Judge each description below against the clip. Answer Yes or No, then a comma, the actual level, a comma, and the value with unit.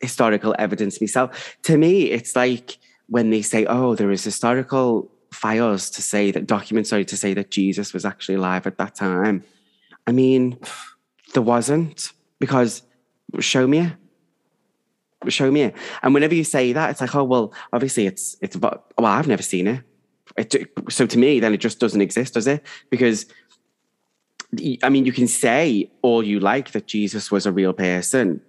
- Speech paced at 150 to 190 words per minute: Yes, average, 175 wpm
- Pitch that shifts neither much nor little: Yes, average, 4.0 semitones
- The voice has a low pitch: Yes, low, 120 Hz